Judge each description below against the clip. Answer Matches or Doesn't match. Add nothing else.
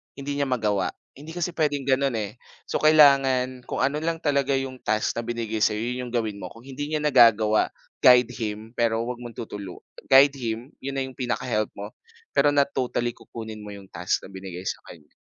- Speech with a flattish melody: Doesn't match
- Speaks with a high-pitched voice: Doesn't match